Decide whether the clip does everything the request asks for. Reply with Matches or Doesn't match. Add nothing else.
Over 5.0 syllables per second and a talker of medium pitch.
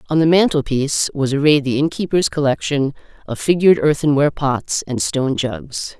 Matches